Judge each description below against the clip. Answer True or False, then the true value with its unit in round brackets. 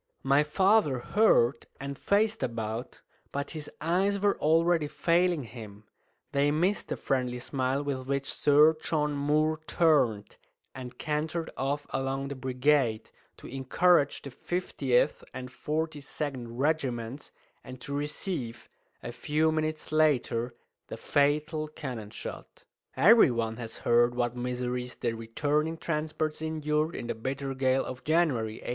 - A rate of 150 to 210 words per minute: False (135 wpm)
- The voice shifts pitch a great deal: False (4.0 semitones)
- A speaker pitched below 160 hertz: True (140 Hz)